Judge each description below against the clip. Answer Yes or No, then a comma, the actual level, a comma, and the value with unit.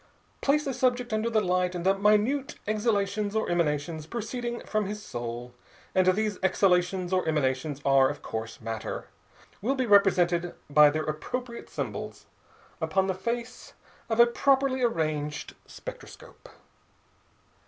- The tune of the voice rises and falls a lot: Yes, wide, 7.0 semitones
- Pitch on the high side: Yes, high, 195 Hz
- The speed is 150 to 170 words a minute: No, slow, 135 wpm